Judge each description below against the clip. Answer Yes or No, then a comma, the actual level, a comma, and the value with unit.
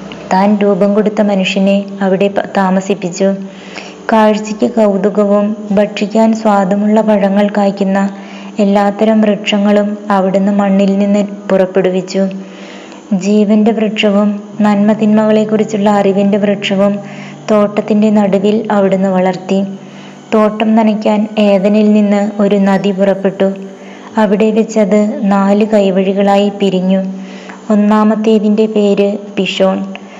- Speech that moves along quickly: No, average, 85 wpm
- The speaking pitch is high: Yes, high, 205 Hz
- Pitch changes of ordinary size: No, narrow, 1.3 semitones